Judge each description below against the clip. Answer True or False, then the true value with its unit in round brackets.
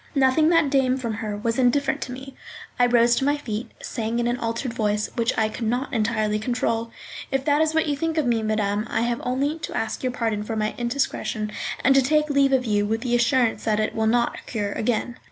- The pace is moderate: False (230 wpm)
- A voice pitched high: True (240 Hz)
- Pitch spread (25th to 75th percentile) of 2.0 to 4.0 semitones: True (3.4 semitones)